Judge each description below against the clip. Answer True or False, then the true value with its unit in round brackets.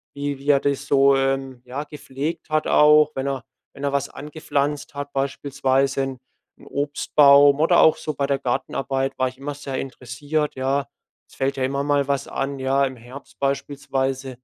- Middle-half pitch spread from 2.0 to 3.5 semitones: False (1.2 semitones)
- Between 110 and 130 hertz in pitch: False (140 Hz)